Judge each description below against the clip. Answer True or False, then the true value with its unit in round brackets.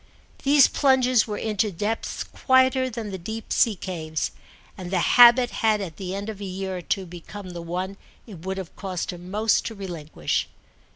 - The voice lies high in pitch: True (195 Hz)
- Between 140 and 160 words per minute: False (185 wpm)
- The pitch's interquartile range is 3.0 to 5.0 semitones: True (3.7 semitones)